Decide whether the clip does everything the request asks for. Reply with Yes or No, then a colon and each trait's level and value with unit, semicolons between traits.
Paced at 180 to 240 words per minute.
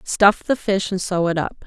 No: fast, 250 wpm